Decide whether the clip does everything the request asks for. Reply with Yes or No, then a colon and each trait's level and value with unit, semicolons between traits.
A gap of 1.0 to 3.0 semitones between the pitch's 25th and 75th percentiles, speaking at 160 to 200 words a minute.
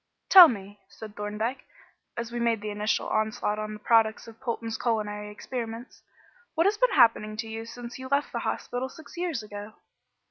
Yes: narrow, 2.6 semitones; average, 180 wpm